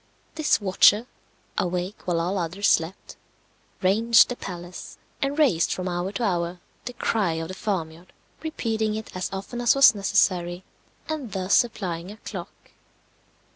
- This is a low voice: No, high, 195 Hz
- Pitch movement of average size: Yes, average, 4.0 semitones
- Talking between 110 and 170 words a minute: Yes, average, 145 wpm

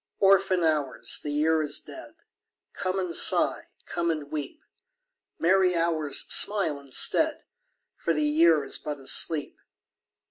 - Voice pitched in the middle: Yes, medium, 160 Hz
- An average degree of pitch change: Yes, average, 3.6 semitones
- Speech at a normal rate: No, slow, 130 wpm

